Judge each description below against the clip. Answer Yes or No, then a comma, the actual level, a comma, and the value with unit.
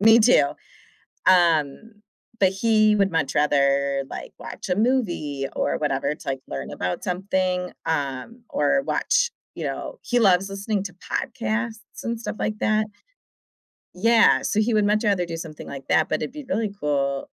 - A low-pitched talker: No, high, 190 Hz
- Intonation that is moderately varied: No, wide, 6.9 semitones